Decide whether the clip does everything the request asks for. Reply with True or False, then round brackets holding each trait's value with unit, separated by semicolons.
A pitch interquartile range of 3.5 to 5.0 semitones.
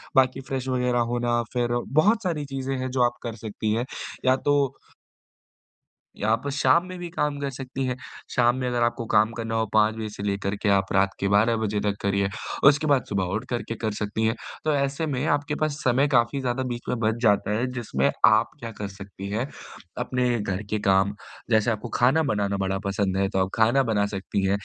True (4.2 semitones)